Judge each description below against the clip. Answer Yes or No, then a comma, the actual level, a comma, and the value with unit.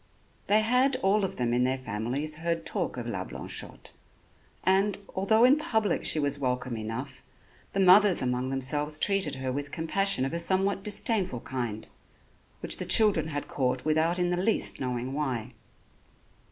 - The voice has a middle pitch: Yes, medium, 155 Hz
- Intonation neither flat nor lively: No, wide, 7.2 semitones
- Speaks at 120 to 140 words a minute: No, average, 165 wpm